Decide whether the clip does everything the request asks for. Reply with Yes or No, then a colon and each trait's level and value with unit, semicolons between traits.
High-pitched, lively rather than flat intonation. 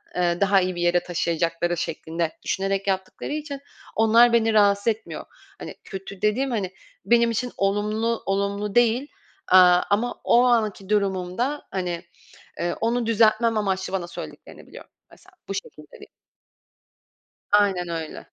No: high, 200 Hz; average, 4.0 semitones